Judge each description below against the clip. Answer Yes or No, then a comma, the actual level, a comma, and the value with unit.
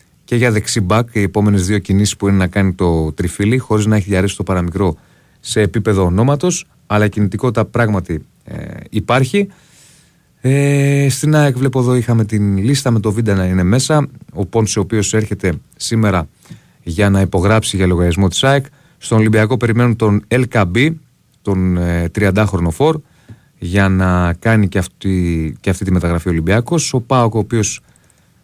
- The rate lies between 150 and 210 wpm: Yes, average, 165 wpm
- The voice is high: No, low, 110 Hz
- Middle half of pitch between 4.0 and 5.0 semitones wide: Yes, average, 4.6 semitones